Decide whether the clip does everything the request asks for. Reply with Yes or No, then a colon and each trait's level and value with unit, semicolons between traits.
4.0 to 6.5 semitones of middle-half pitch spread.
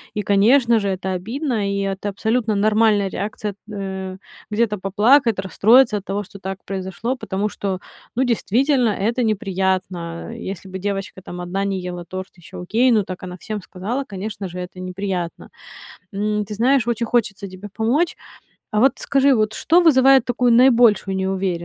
No: average, 3.5 semitones